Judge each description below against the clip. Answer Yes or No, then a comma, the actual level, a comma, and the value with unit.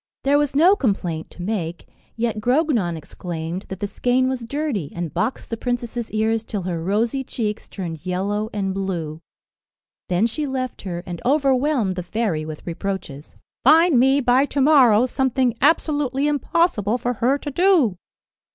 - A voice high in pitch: Yes, high, 230 Hz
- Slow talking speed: No, average, 160 wpm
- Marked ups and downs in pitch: Yes, wide, 6.3 semitones